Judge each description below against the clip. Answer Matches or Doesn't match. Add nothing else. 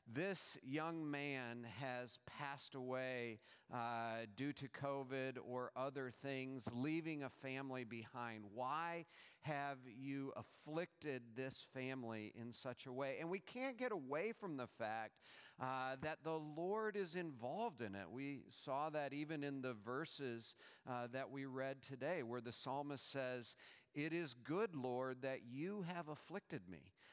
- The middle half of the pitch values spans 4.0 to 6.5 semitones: Doesn't match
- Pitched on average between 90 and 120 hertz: Doesn't match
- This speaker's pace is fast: Doesn't match